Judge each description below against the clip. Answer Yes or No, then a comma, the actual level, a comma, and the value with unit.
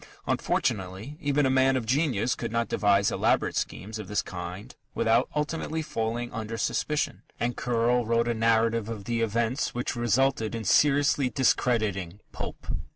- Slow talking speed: No, average, 155 wpm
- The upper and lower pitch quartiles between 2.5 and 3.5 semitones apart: Yes, average, 3.1 semitones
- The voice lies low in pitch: Yes, low, 115 Hz